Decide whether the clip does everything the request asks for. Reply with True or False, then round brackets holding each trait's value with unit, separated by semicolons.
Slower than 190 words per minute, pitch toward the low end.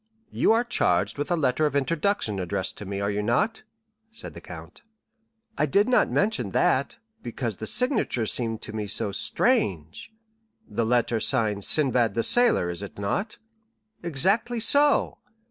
True (160 wpm; 125 Hz)